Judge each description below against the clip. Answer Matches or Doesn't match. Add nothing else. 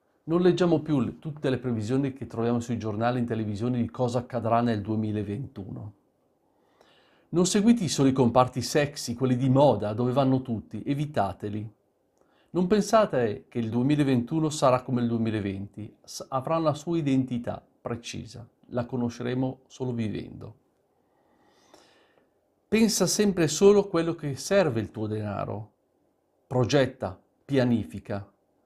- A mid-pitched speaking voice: Doesn't match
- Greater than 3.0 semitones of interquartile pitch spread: Matches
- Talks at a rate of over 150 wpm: Doesn't match